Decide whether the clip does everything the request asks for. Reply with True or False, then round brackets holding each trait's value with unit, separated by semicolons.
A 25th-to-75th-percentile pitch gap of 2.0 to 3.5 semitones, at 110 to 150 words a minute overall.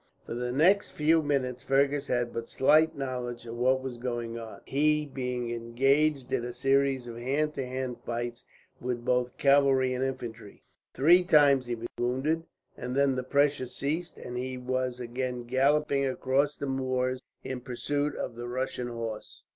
False (2.4 semitones; 170 wpm)